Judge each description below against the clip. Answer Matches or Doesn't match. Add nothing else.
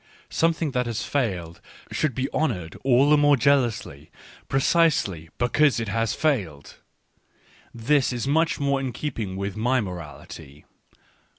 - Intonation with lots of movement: Matches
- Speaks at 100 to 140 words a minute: Matches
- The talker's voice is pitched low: Matches